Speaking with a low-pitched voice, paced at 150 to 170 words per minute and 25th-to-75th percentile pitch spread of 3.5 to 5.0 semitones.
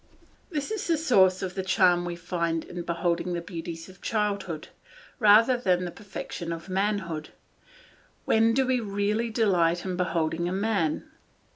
No: medium, 185 Hz; average, 155 wpm; average, 3.8 semitones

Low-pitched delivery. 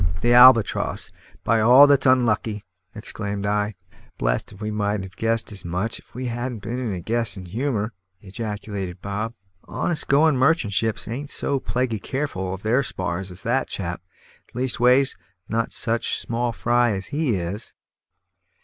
Yes: low, 115 Hz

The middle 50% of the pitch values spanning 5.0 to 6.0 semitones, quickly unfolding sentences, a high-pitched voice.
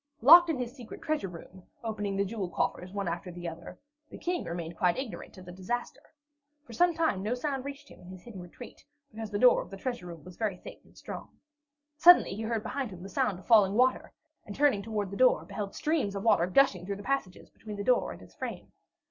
Yes: wide, 5.5 semitones; fast, 230 wpm; high, 210 Hz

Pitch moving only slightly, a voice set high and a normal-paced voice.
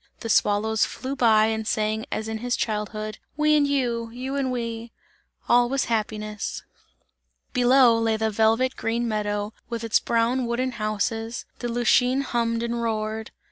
Yes: narrow, 2.0 semitones; high, 230 Hz; average, 160 wpm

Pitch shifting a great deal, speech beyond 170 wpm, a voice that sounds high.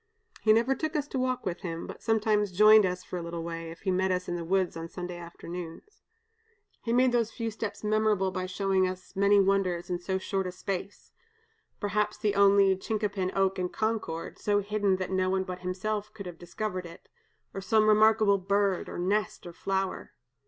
No: average, 2.7 semitones; average, 200 wpm; high, 195 Hz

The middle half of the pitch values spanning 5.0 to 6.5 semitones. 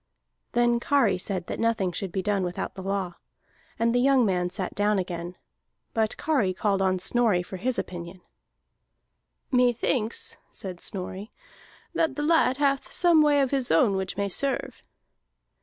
Yes: average, 5.3 semitones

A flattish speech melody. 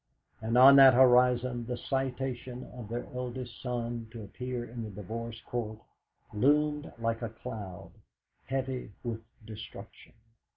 Yes: narrow, 2.1 semitones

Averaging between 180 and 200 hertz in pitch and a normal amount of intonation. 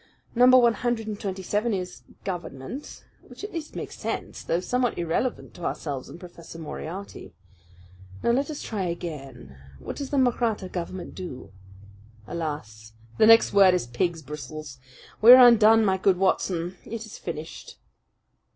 No: medium, 185 Hz; wide, 5.9 semitones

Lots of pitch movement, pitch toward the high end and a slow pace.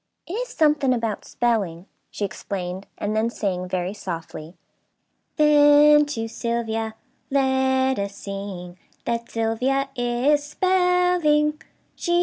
Yes: wide, 6.7 semitones; high, 235 Hz; slow, 110 wpm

